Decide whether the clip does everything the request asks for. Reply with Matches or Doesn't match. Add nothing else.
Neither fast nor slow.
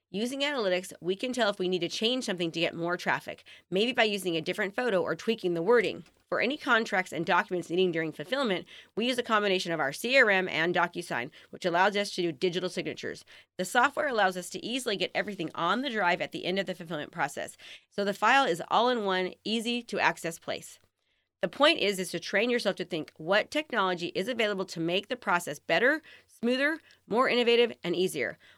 Doesn't match